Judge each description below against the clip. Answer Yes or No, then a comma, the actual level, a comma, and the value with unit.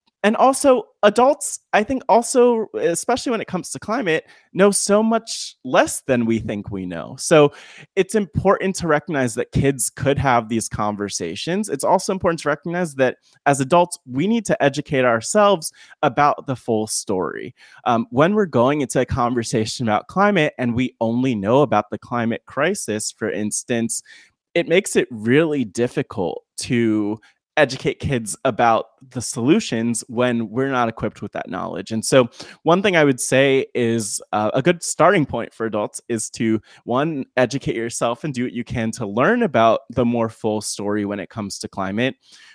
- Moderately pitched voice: No, low, 130 Hz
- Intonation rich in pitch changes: Yes, wide, 7.2 semitones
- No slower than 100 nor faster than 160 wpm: No, average, 175 wpm